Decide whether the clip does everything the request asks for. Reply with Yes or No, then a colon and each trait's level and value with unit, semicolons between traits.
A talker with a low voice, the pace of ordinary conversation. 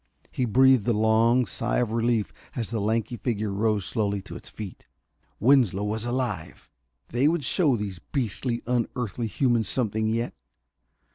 Yes: low, 115 Hz; average, 150 wpm